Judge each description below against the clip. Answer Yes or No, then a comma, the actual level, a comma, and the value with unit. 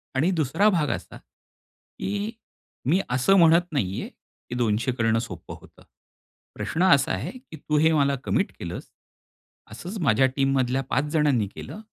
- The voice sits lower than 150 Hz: Yes, medium, 140 Hz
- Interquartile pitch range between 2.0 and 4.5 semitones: No, average, 5.0 semitones